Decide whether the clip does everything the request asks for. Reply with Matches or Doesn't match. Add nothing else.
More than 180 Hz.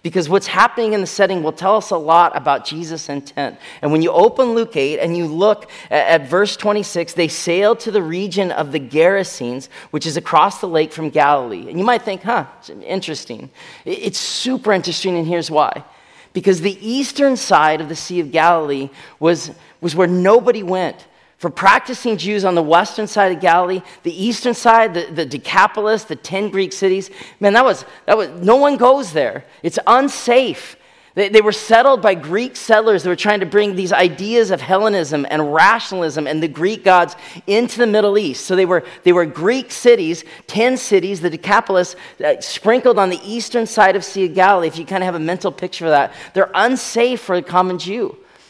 Matches